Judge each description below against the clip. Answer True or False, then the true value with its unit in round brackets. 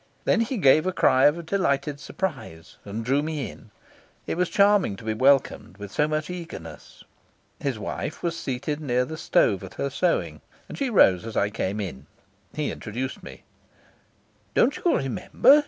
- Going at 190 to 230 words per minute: False (170 wpm)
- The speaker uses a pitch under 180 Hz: True (140 Hz)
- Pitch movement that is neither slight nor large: False (7.8 semitones)